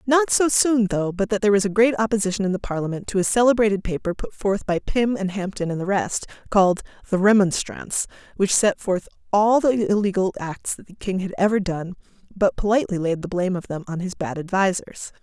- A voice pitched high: Yes, high, 200 Hz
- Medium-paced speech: No, fast, 215 wpm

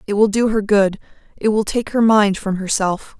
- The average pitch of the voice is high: Yes, high, 205 Hz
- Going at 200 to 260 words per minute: Yes, fast, 205 wpm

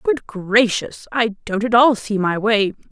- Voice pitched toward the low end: No, high, 220 Hz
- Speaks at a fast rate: No, average, 185 wpm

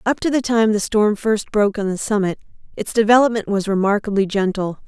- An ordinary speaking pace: Yes, average, 195 wpm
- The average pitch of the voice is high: Yes, high, 210 Hz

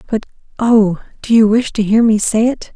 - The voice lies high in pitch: Yes, high, 220 Hz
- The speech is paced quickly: No, average, 175 wpm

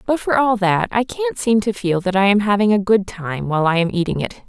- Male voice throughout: No, female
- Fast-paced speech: Yes, fast, 280 wpm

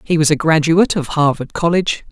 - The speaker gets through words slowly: No, average, 200 wpm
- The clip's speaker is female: No, male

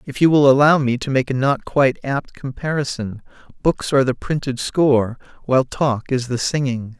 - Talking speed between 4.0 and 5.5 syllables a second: Yes, 5.2 syllables/s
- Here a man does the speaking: Yes, male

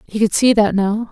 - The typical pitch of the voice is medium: No, high, 215 Hz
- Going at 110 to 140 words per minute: No, fast, 270 wpm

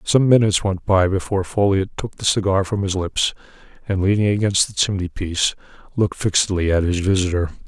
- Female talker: No, male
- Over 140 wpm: Yes, average, 170 wpm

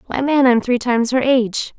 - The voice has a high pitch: Yes, high, 245 Hz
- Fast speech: Yes, fast, 235 wpm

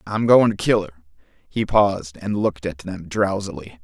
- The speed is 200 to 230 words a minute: Yes, fast, 205 wpm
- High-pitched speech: No, low, 100 Hz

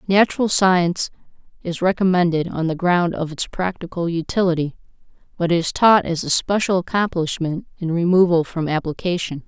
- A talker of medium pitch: Yes, medium, 175 Hz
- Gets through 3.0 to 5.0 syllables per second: No, 5.2 syllables/s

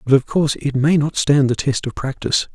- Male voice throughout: Yes, male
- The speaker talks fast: Yes, fast, 260 wpm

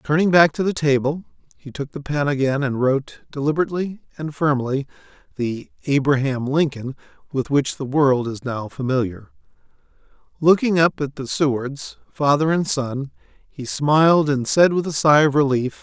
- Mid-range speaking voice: Yes, medium, 145 Hz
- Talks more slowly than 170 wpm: Yes, average, 160 wpm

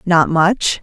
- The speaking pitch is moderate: Yes, medium, 175 Hz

